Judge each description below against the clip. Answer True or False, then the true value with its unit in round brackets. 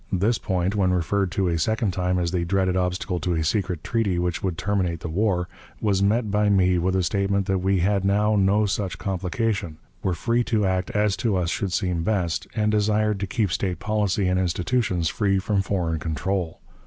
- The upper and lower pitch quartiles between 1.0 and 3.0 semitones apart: True (2.6 semitones)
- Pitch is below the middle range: True (95 Hz)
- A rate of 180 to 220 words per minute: True (205 wpm)